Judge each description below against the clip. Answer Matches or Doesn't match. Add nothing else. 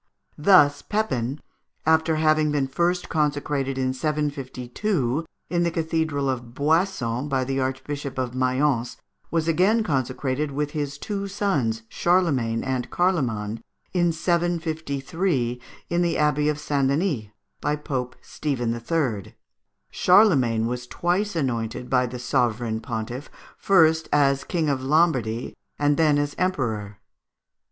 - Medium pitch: Matches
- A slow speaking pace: Matches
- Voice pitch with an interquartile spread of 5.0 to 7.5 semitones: Doesn't match